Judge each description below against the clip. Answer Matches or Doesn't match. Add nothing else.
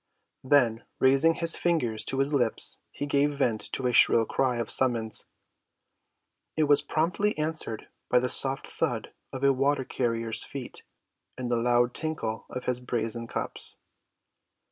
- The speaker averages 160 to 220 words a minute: Doesn't match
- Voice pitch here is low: Matches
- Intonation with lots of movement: Doesn't match